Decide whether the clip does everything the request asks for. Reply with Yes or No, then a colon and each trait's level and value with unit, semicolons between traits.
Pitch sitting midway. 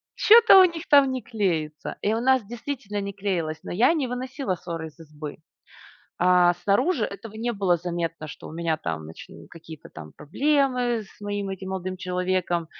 No: high, 195 Hz